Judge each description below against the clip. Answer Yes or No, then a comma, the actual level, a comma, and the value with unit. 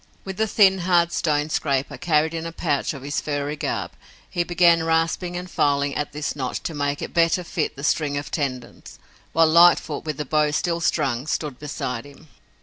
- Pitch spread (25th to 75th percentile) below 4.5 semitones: Yes, average, 2.9 semitones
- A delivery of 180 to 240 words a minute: Yes, average, 195 wpm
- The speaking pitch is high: No, medium, 155 Hz